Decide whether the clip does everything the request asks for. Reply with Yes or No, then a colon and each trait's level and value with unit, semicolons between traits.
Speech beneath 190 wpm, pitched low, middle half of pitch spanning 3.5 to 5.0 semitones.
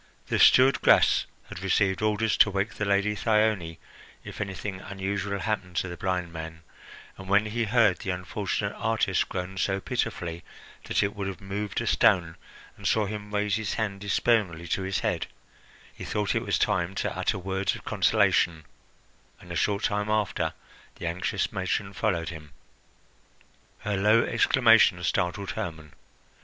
No: average, 160 wpm; low, 100 Hz; average, 2.7 semitones